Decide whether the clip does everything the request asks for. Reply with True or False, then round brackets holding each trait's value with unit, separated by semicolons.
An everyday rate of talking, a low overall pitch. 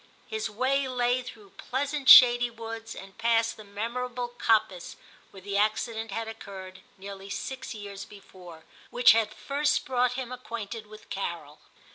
False (150 wpm; 225 Hz)